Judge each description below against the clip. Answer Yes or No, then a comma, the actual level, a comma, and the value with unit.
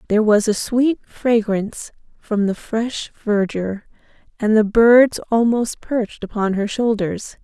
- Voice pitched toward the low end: No, high, 220 Hz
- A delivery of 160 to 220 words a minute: No, slow, 135 wpm